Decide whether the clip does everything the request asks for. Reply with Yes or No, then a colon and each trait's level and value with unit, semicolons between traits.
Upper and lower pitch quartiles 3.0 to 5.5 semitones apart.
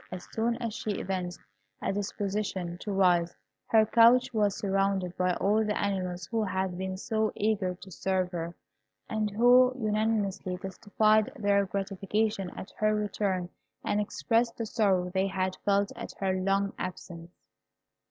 No: narrow, 2.4 semitones